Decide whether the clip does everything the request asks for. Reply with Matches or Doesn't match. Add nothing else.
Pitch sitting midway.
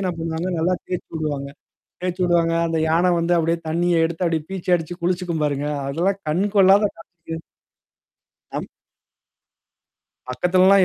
Matches